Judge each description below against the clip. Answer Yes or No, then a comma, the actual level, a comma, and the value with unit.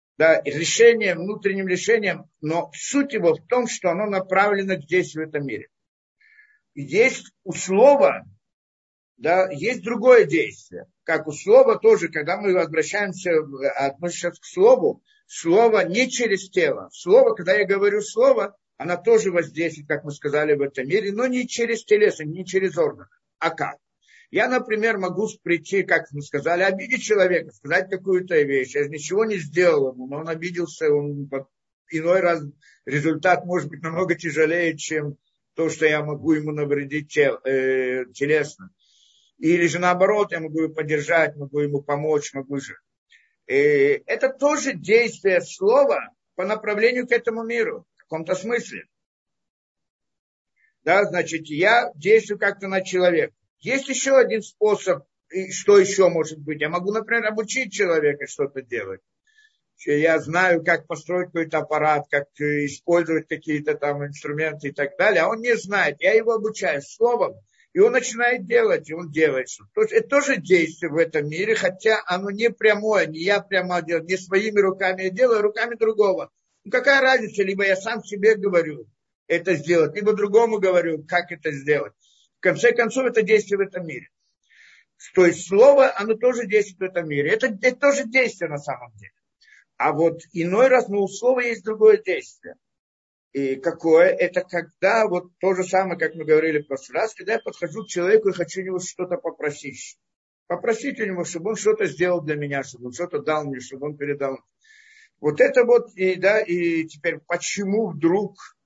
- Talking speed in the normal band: No, fast, 165 wpm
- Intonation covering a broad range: Yes, wide, 6.5 semitones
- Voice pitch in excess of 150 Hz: Yes, medium, 185 Hz